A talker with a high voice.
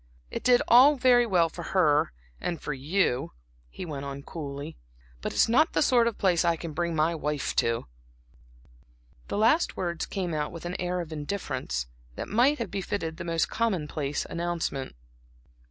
No: medium, 170 Hz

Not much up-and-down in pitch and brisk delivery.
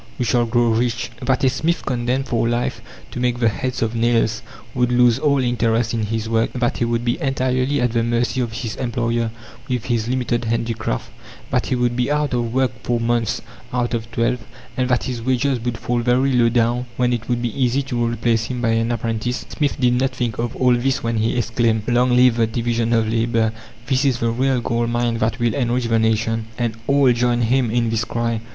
Yes: narrow, 1.4 semitones; fast, 220 wpm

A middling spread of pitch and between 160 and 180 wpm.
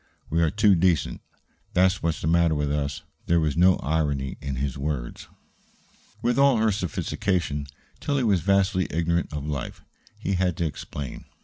Yes: average, 4.3 semitones; average, 165 wpm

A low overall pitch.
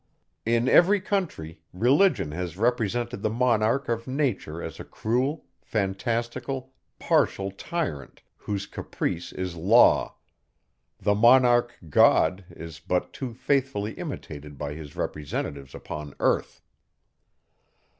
Yes: low, 110 Hz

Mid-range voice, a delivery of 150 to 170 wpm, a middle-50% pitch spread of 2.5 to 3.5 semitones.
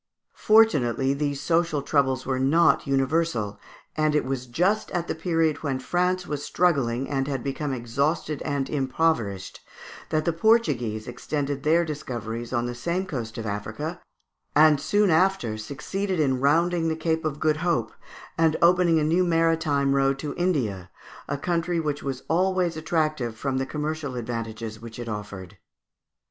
No: medium, 145 Hz; average, 155 wpm; average, 4.6 semitones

